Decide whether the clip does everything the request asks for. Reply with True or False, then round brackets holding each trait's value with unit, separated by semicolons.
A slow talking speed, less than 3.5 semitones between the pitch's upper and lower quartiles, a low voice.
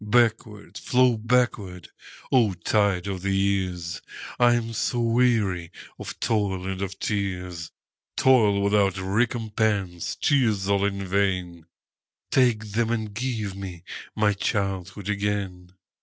True (110 wpm; 2.9 semitones; 100 Hz)